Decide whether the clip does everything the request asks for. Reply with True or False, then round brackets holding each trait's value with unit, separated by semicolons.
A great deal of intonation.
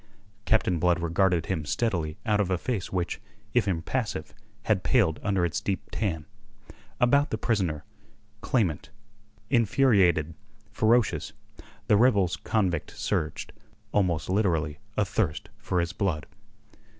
False (4.6 semitones)